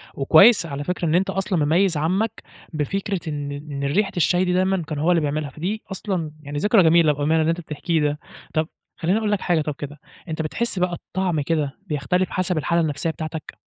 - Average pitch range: Yes, average, 3.7 semitones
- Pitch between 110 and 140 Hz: No, medium, 165 Hz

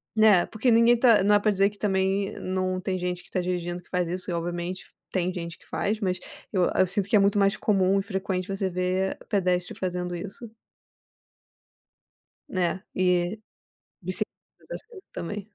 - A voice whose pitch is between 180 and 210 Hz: Yes, high, 190 Hz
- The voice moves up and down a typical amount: No, narrow, 2.0 semitones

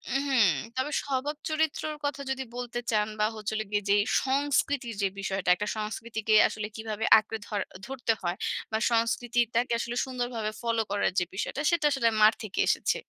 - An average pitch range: Yes, average, 3.6 semitones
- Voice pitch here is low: No, high, 230 Hz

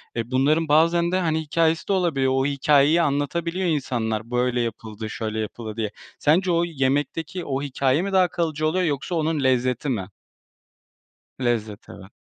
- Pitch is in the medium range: Yes, medium, 145 Hz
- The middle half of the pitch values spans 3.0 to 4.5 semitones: No, average, 5.2 semitones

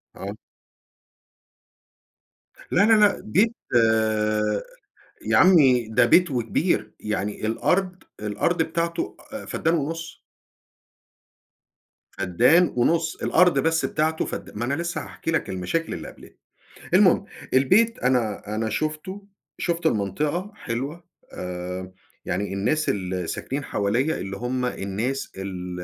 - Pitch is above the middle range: No, low, 130 Hz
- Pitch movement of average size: No, wide, 7.8 semitones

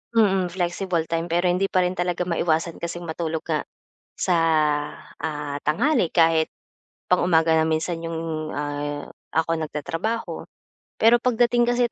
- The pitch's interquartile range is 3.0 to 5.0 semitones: No, narrow, 2.5 semitones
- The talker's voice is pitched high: No, medium, 170 Hz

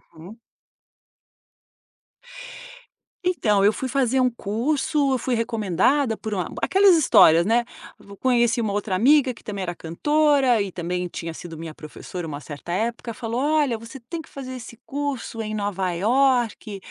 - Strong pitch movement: Yes, wide, 5.7 semitones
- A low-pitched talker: No, high, 230 Hz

